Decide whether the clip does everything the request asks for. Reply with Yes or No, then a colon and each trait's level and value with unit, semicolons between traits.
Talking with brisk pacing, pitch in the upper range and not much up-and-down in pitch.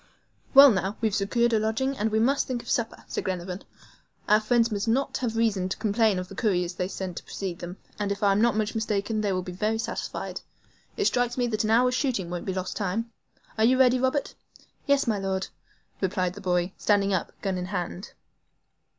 No: fast, 210 wpm; high, 210 Hz; average, 3.6 semitones